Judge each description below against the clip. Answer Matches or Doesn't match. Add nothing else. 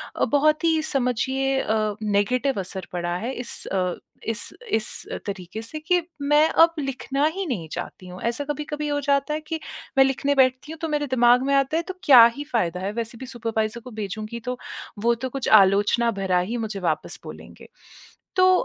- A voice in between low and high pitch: Doesn't match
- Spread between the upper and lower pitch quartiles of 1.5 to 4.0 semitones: Doesn't match